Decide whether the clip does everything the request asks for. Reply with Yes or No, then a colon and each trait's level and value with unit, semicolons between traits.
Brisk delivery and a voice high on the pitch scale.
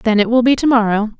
Yes: fast, 300 wpm; high, 230 Hz